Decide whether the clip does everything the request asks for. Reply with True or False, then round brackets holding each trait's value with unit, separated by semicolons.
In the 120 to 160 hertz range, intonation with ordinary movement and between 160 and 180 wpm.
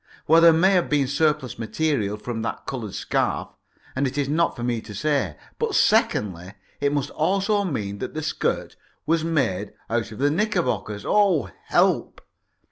False (140 Hz; 6.6 semitones; 170 wpm)